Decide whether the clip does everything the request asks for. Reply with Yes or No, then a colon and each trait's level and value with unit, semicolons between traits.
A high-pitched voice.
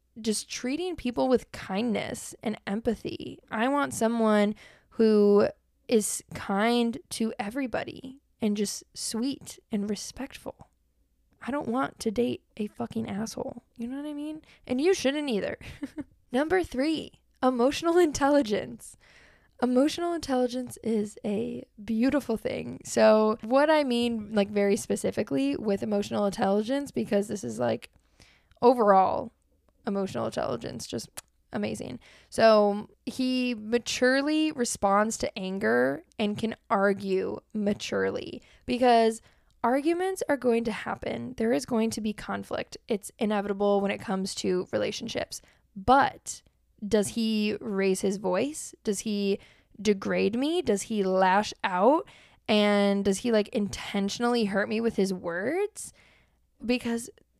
Yes: high, 225 Hz